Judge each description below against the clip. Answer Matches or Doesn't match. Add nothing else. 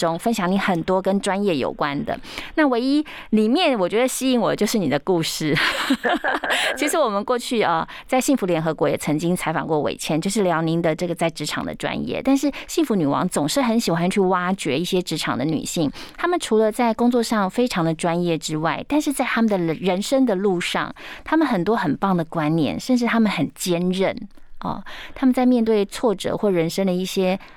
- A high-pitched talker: Matches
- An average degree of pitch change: Doesn't match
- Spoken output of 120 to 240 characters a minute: Doesn't match